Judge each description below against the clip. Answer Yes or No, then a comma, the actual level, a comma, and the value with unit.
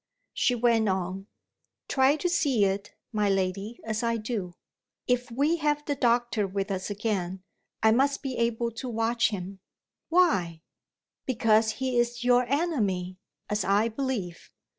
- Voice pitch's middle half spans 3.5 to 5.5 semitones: Yes, average, 4.1 semitones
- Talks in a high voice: Yes, high, 230 Hz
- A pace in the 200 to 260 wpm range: No, average, 145 wpm